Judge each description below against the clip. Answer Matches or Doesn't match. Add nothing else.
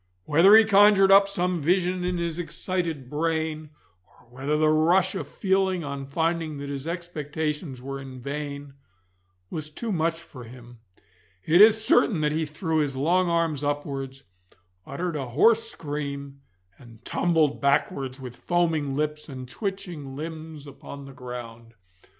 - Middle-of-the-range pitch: Matches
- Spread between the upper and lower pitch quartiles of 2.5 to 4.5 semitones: Matches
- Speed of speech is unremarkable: Matches